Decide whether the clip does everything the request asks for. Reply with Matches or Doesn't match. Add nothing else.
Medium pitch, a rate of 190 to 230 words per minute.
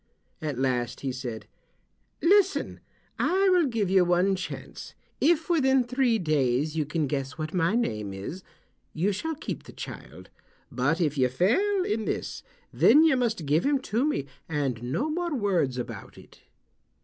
Doesn't match